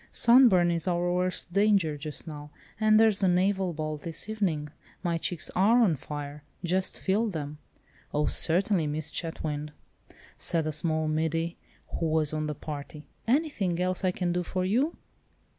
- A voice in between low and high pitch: Yes, medium, 175 Hz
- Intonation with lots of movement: No, average, 3.8 semitones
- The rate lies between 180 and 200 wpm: No, average, 160 wpm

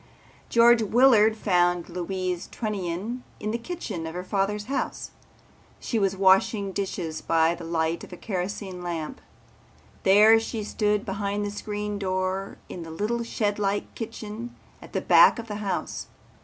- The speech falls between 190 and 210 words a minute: No, average, 150 wpm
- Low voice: No, high, 200 Hz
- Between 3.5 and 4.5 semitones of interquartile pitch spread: No, average, 3.0 semitones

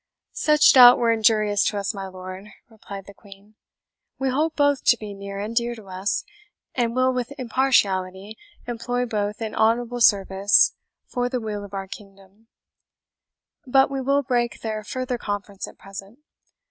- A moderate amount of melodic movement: Yes, average, 3.8 semitones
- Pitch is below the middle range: No, high, 220 Hz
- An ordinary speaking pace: Yes, average, 160 wpm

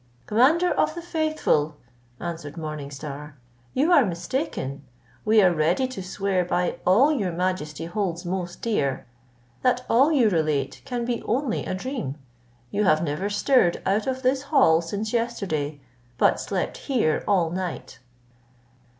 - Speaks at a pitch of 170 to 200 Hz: Yes, high, 190 Hz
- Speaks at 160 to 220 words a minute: No, average, 145 wpm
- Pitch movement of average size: No, wide, 7.7 semitones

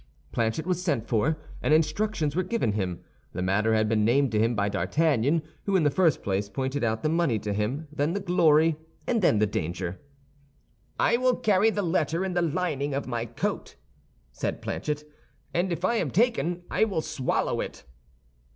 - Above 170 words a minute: Yes, average, 190 wpm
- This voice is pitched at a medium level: Yes, medium, 150 Hz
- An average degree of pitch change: No, wide, 8.0 semitones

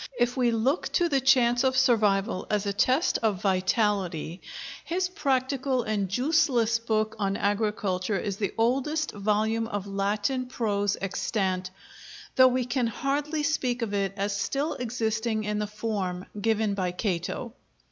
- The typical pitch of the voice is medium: No, high, 220 Hz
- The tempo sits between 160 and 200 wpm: No, average, 150 wpm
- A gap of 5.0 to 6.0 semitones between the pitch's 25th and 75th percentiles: No, average, 4.1 semitones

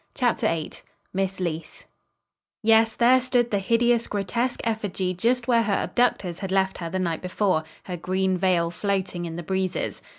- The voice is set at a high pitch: Yes, high, 195 Hz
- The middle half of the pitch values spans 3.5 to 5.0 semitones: Yes, average, 4.2 semitones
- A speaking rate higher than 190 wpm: No, average, 165 wpm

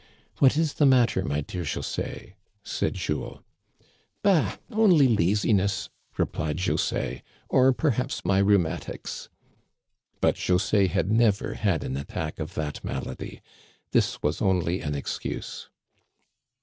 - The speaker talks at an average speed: No, slow, 125 wpm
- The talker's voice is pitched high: No, low, 100 Hz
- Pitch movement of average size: No, wide, 6.9 semitones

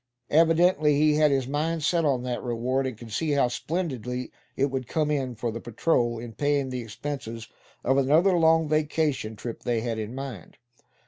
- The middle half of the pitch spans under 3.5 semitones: No, average, 4.2 semitones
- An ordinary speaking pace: Yes, average, 185 wpm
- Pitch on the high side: No, low, 135 Hz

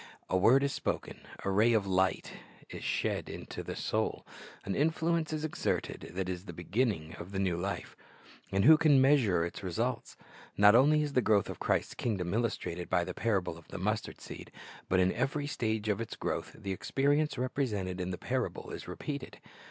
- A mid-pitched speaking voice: No, low, 105 Hz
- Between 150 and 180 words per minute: No, average, 190 wpm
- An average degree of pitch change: No, wide, 6.5 semitones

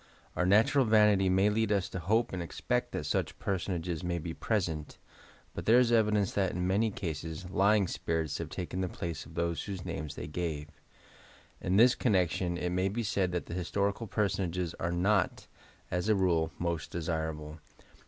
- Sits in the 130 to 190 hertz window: No, very low, 90 Hz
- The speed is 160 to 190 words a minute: Yes, average, 175 wpm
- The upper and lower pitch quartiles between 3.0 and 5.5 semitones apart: Yes, average, 3.3 semitones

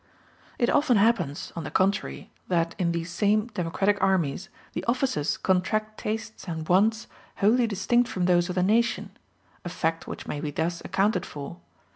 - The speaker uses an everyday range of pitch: Yes, average, 4.2 semitones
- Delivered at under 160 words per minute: No, average, 165 wpm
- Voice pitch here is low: No, high, 190 Hz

